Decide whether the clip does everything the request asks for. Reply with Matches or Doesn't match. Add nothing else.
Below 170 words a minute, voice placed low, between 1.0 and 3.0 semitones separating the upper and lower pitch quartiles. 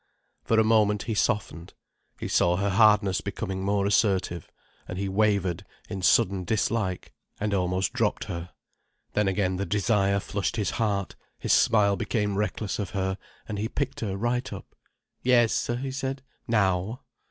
Matches